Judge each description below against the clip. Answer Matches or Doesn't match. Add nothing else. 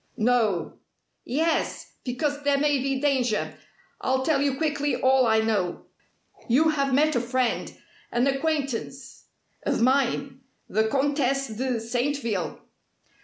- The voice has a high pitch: Matches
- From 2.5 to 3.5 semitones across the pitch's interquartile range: Matches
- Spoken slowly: Matches